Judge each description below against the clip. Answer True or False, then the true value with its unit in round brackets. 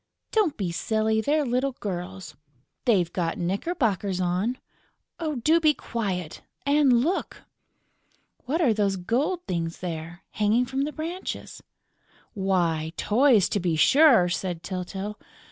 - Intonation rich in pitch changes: True (7.2 semitones)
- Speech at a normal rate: False (125 wpm)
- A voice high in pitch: True (210 Hz)